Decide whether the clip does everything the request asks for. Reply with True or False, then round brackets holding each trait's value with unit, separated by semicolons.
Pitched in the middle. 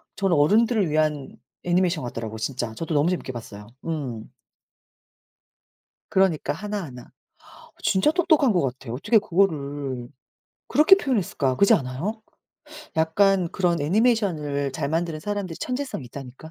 True (160 Hz)